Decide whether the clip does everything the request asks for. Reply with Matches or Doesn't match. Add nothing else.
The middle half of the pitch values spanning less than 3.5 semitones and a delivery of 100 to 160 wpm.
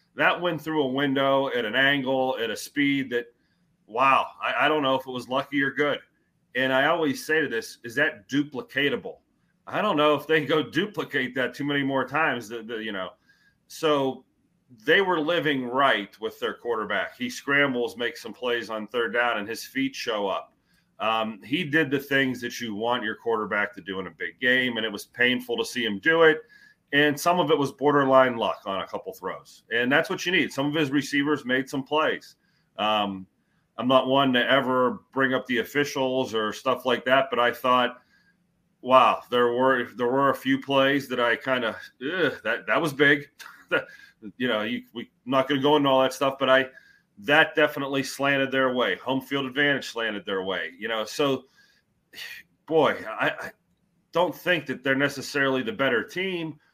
Doesn't match